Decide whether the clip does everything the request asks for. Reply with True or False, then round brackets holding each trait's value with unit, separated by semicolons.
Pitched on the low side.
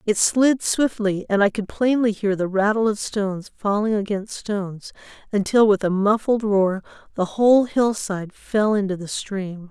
False (205 Hz)